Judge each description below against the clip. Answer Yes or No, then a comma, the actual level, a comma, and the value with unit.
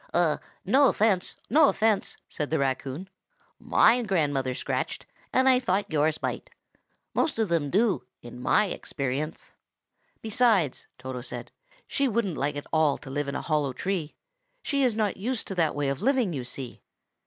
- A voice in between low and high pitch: Yes, medium, 170 Hz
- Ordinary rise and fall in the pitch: No, wide, 7.8 semitones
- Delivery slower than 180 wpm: Yes, average, 165 wpm